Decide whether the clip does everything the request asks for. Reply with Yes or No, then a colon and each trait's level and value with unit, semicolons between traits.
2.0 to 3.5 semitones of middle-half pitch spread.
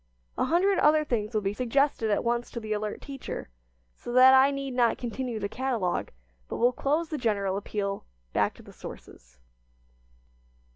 No: average, 4.5 semitones